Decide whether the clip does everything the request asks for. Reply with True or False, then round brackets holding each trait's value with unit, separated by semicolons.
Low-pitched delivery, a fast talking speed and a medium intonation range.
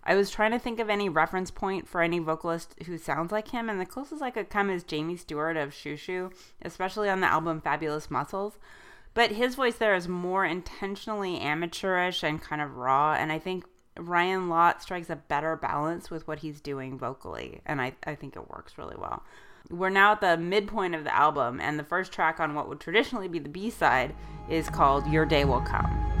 False (175 Hz; 215 wpm; 4.0 semitones)